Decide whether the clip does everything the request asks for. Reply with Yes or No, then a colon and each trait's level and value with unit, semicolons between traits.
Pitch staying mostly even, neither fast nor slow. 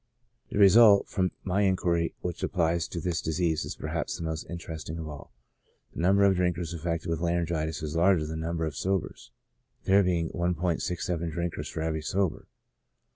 Yes: narrow, 2.1 semitones; average, 180 wpm